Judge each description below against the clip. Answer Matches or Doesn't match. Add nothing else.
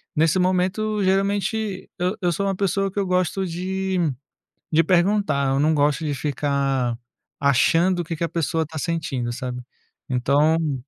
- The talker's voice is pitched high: Doesn't match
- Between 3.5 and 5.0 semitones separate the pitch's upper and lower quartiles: Matches